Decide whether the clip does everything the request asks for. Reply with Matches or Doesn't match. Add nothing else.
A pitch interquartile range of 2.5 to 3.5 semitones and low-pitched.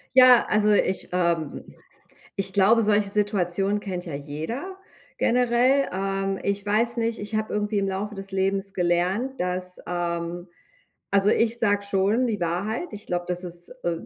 Doesn't match